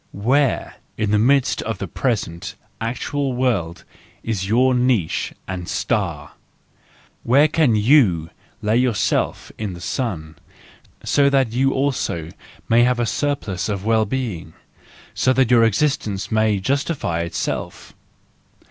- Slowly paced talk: Yes, slow, 125 wpm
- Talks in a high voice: No, low, 115 Hz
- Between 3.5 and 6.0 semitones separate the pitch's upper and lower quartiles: Yes, average, 5.2 semitones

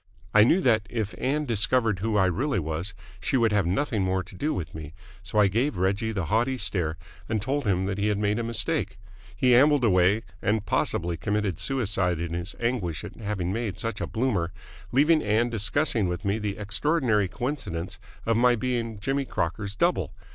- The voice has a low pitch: Yes, low, 105 Hz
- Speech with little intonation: No, average, 4.2 semitones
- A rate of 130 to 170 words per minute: No, average, 190 wpm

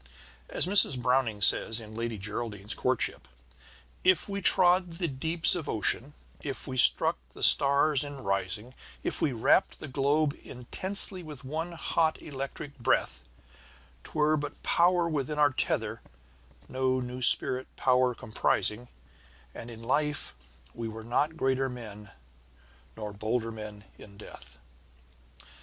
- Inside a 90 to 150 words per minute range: Yes, slow, 135 wpm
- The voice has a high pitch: No, low, 130 Hz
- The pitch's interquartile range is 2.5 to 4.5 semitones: No, average, 5.1 semitones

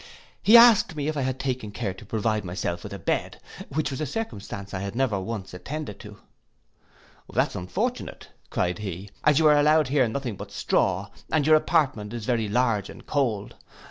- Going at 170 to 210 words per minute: Yes, average, 190 wpm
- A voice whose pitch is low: Yes, low, 120 Hz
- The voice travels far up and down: Yes, wide, 6.5 semitones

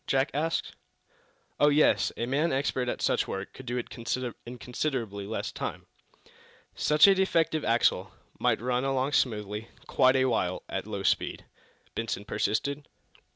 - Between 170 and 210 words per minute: No, average, 150 wpm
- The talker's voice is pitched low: Yes, low, 125 Hz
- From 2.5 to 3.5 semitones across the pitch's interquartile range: No, average, 4.5 semitones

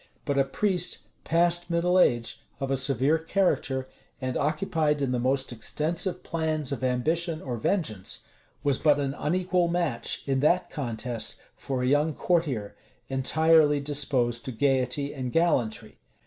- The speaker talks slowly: No, average, 145 wpm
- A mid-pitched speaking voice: Yes, medium, 145 Hz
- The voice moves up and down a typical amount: Yes, average, 4.2 semitones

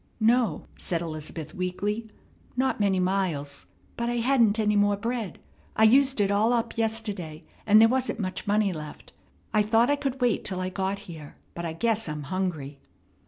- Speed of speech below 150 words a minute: No, average, 175 wpm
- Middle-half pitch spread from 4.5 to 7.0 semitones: No, average, 4.0 semitones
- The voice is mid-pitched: No, high, 205 Hz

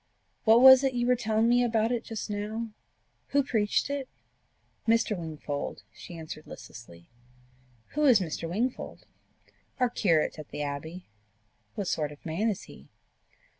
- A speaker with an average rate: Yes, average, 150 wpm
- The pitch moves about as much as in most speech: No, wide, 7.1 semitones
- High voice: Yes, high, 215 Hz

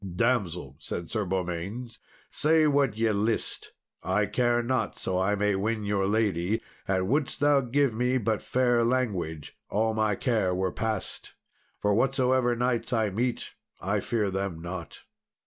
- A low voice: Yes, low, 110 Hz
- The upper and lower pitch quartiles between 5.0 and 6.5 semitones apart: No, average, 4.3 semitones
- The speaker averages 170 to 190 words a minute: No, average, 150 wpm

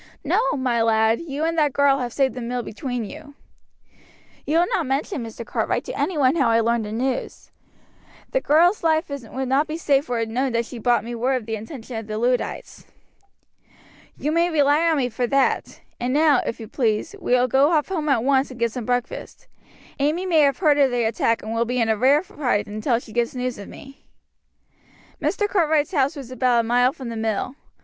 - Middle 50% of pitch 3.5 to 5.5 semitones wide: Yes, average, 4.1 semitones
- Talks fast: Yes, fast, 220 wpm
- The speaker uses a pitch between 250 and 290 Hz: Yes, very high, 255 Hz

